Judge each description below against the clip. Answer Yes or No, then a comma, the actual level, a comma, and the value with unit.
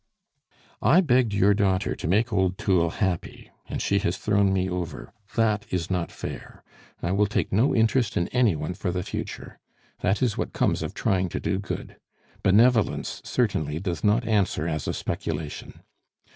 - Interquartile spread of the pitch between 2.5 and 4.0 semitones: Yes, average, 3.4 semitones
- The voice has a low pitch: Yes, very low, 95 Hz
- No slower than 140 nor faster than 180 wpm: Yes, average, 170 wpm